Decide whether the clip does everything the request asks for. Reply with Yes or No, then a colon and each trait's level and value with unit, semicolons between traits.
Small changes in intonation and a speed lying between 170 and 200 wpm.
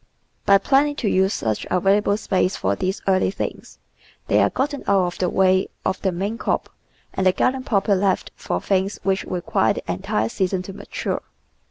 Yes: narrow, 1.5 semitones; average, 185 wpm